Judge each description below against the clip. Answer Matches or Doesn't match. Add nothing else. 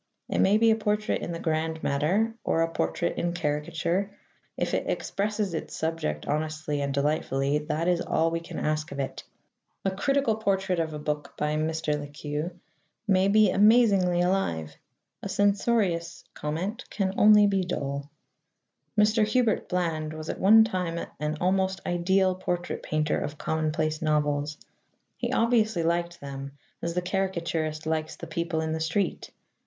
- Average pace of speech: Matches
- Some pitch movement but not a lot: Matches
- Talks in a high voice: Doesn't match